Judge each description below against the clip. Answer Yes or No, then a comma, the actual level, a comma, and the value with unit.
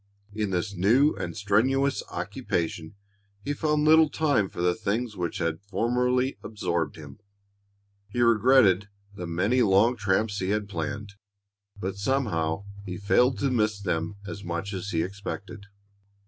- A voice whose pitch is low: Yes, low, 100 Hz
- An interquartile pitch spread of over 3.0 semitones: Yes, average, 4.9 semitones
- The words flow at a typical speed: Yes, average, 145 wpm